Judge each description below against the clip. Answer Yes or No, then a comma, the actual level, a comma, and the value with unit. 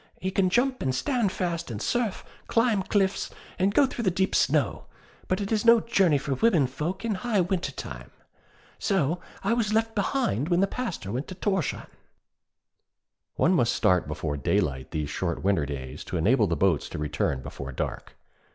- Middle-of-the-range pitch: Yes, medium, 180 Hz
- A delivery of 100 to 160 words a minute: No, average, 180 wpm